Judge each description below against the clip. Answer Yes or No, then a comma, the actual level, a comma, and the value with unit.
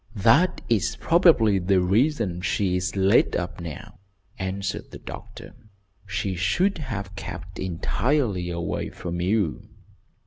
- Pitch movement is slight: No, average, 3.8 semitones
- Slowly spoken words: Yes, slow, 125 wpm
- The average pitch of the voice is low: Yes, very low, 95 Hz